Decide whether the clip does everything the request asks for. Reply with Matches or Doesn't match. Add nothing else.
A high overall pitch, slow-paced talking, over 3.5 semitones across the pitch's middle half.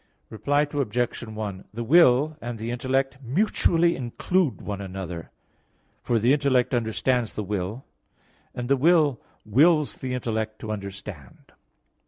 Doesn't match